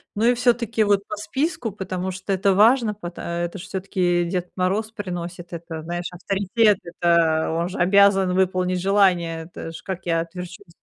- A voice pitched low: No, medium, 185 Hz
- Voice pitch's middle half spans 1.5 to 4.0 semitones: Yes, average, 2.8 semitones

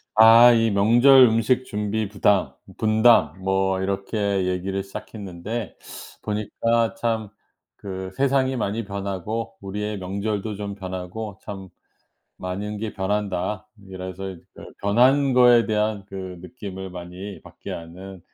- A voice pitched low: Yes, low, 100 Hz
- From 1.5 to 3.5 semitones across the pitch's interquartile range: Yes, average, 2.7 semitones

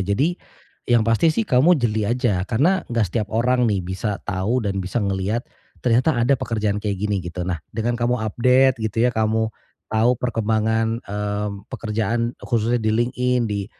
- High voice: No, low, 115 Hz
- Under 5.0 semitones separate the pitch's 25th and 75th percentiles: Yes, average, 2.9 semitones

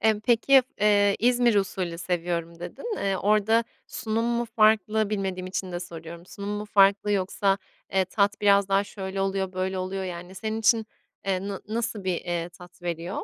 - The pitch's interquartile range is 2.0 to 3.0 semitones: Yes, narrow, 2.5 semitones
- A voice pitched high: Yes, high, 195 Hz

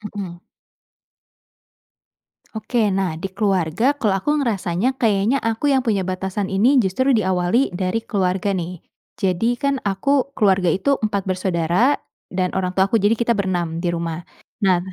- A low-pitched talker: No, high, 195 Hz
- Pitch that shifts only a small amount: No, average, 4.0 semitones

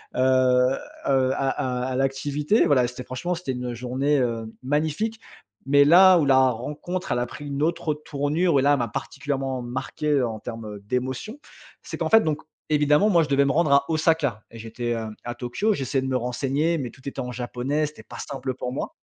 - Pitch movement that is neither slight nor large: Yes, average, 3.2 semitones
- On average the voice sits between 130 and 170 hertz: Yes, low, 135 Hz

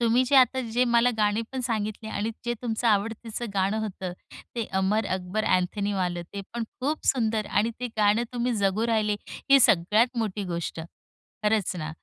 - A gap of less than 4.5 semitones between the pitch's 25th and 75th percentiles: Yes, average, 2.8 semitones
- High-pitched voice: Yes, high, 220 Hz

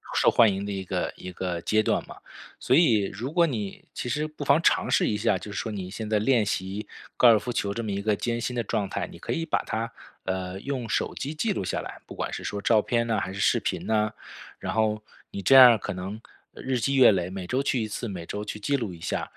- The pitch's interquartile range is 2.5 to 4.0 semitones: Yes, average, 3.7 semitones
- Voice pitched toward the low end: Yes, low, 110 Hz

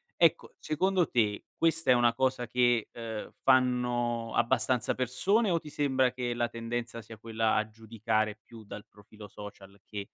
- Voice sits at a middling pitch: No, low, 120 Hz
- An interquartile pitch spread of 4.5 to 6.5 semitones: No, average, 2.7 semitones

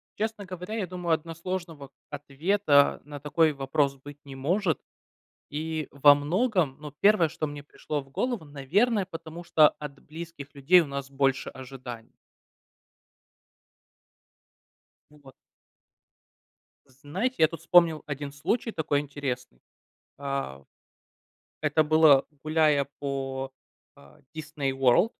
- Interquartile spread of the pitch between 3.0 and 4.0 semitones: Yes, average, 3.5 semitones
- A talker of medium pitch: Yes, medium, 150 Hz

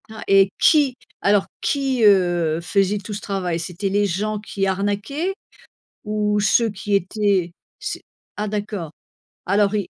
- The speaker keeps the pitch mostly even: Yes, narrow, 1.7 semitones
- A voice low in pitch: No, high, 205 Hz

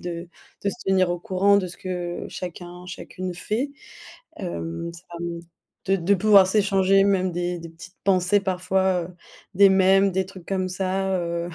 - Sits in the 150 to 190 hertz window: Yes, medium, 185 Hz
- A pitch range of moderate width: No, narrow, 1.8 semitones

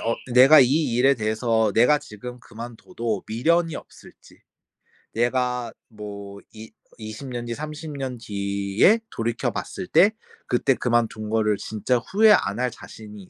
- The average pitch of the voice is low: Yes, low, 120 Hz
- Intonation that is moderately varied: Yes, average, 3.7 semitones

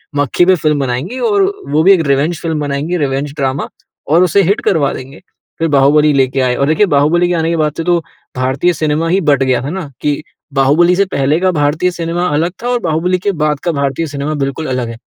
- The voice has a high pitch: No, medium, 150 Hz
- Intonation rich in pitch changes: No, average, 3.8 semitones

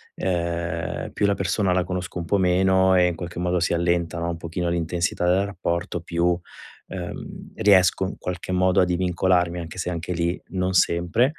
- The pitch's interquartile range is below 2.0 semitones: Yes, narrow, 1.4 semitones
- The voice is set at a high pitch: No, very low, 90 Hz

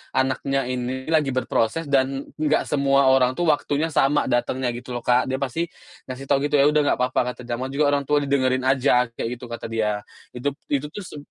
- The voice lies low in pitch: Yes, low, 130 Hz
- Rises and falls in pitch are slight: Yes, narrow, 2.3 semitones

